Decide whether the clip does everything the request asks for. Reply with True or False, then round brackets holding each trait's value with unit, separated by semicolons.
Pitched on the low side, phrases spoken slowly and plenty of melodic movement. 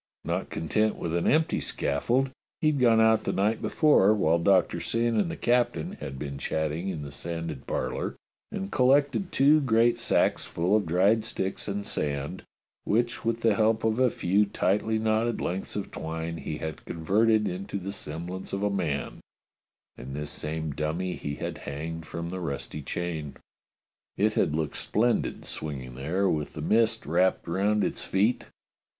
False (95 Hz; 170 wpm; 5.8 semitones)